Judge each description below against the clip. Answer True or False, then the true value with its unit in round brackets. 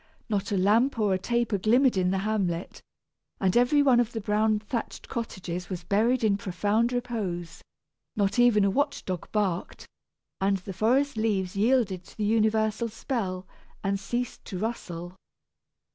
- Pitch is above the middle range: True (210 Hz)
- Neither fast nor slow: True (160 wpm)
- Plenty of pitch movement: False (3.7 semitones)